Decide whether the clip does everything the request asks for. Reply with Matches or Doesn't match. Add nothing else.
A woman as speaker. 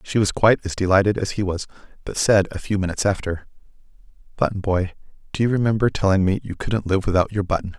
Doesn't match